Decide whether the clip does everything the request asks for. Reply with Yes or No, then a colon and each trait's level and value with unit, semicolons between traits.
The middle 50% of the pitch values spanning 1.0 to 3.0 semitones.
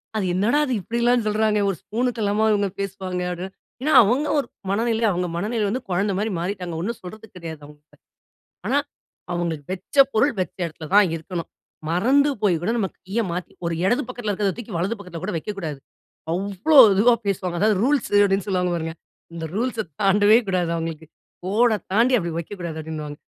No: average, 4.0 semitones